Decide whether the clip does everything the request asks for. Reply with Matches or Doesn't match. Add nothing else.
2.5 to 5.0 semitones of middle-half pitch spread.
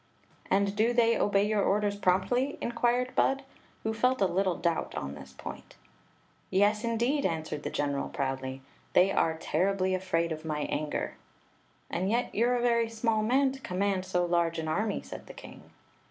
Doesn't match